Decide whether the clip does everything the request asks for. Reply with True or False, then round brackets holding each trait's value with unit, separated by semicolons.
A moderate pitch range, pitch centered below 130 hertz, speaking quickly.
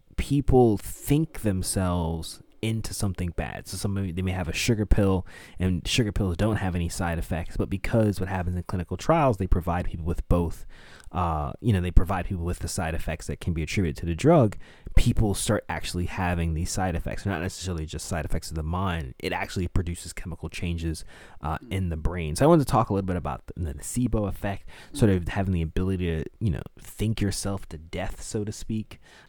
True (3.0 semitones; 90 Hz; 210 wpm)